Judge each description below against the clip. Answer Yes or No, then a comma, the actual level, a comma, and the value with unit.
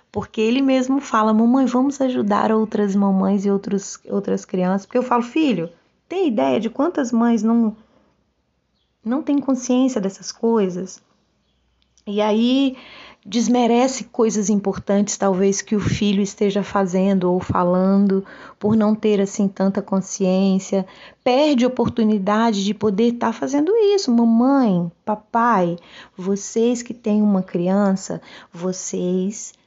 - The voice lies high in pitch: Yes, high, 215 Hz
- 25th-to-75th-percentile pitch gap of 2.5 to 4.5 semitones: Yes, average, 3.7 semitones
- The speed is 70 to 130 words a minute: Yes, average, 125 wpm